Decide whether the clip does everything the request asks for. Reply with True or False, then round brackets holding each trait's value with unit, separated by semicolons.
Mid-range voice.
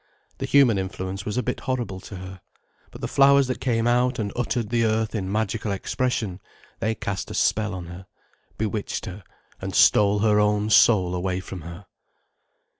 False (105 Hz)